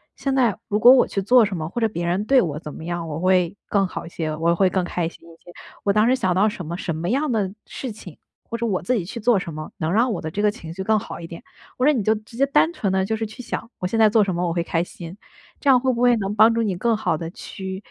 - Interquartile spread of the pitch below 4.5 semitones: No, average, 4.9 semitones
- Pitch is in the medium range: No, high, 200 Hz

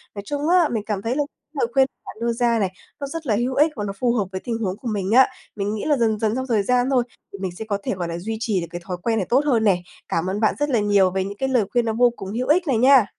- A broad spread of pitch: No, average, 4.4 semitones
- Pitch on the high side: Yes, high, 225 Hz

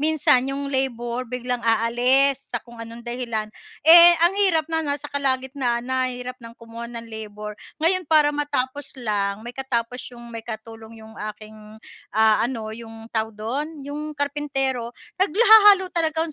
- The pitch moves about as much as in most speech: Yes, average, 4.1 semitones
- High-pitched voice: Yes, very high, 250 Hz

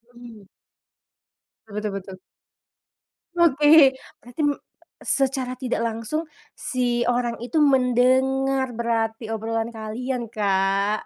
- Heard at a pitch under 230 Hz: No, high, 240 Hz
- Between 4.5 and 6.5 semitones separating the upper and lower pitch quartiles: No, average, 3.0 semitones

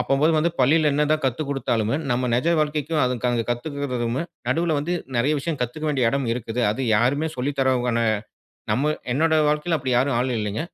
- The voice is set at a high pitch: No, low, 135 Hz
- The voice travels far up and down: No, average, 3.8 semitones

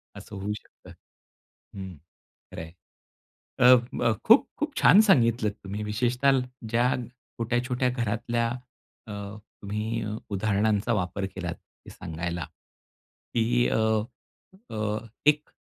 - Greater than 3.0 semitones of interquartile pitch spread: Yes, average, 3.5 semitones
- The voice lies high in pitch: No, low, 110 Hz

